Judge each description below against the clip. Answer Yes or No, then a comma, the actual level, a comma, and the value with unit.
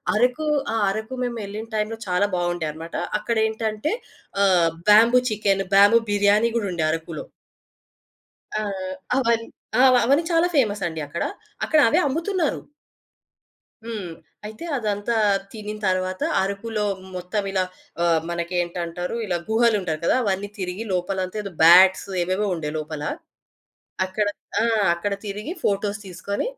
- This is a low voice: No, high, 205 Hz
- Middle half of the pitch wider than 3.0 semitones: Yes, average, 3.6 semitones